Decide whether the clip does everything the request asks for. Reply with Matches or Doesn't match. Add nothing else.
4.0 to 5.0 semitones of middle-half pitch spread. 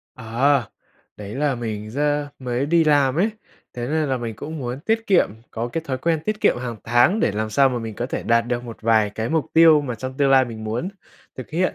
Matches